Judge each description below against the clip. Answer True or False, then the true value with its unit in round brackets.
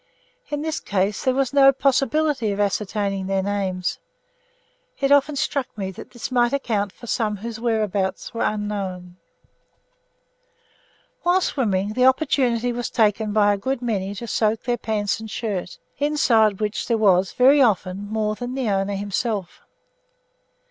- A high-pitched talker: True (220 Hz)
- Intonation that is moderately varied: True (4.2 semitones)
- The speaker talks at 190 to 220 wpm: False (150 wpm)